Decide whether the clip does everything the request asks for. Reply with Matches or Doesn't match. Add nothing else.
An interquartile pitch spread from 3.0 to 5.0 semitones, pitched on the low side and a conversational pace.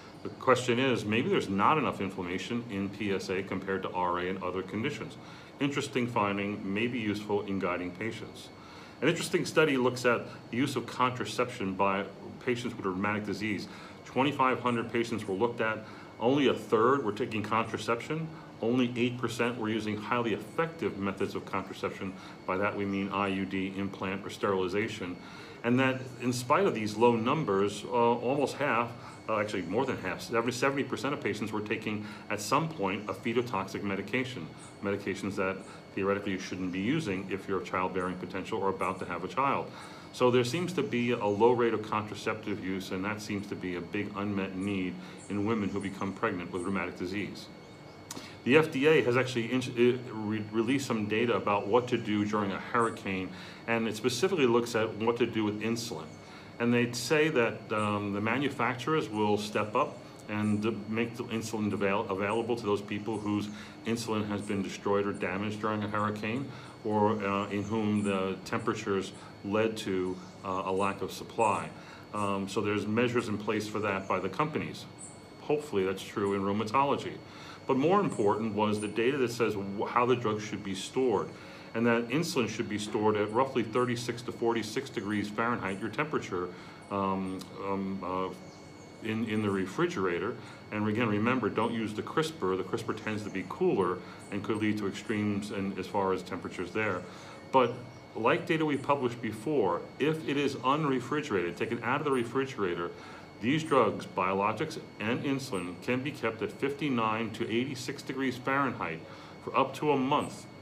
Matches